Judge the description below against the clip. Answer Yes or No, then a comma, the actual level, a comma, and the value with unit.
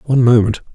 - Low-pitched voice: Yes, low, 120 Hz